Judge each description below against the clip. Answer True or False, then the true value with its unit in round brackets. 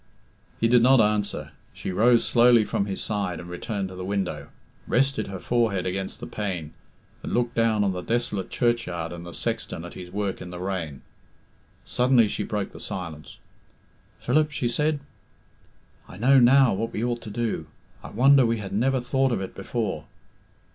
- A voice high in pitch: False (105 Hz)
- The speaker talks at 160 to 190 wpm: True (180 wpm)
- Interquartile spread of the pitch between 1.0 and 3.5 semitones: False (4.6 semitones)